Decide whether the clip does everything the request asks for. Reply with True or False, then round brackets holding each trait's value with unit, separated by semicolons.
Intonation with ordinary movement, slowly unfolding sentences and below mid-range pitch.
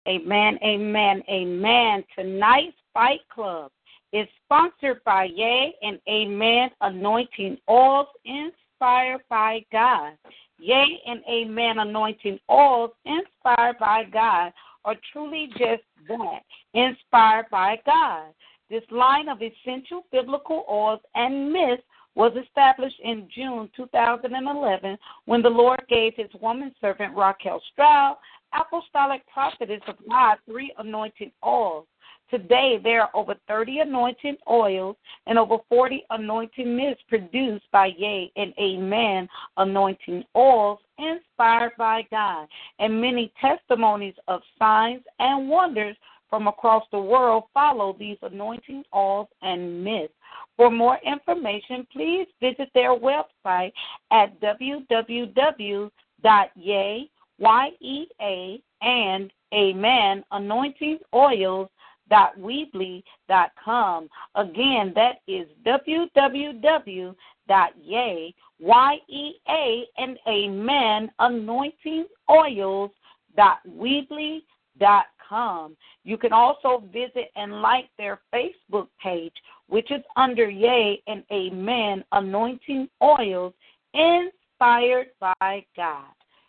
False (4.4 semitones; 105 wpm; 230 Hz)